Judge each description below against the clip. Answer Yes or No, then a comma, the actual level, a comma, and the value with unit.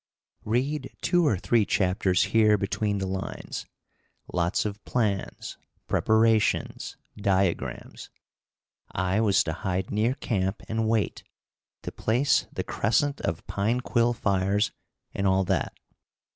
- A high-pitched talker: No, low, 105 Hz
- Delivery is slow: Yes, slow, 120 wpm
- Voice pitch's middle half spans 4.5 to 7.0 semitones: No, average, 2.9 semitones